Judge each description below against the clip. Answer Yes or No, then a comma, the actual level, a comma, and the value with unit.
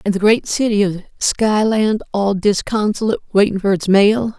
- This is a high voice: Yes, high, 205 Hz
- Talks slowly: No, average, 165 wpm